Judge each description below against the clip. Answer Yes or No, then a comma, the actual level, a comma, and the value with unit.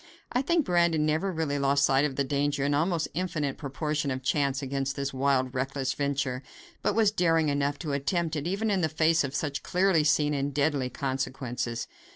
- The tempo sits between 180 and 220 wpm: Yes, average, 190 wpm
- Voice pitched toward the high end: No, medium, 145 Hz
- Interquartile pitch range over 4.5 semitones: No, average, 2.9 semitones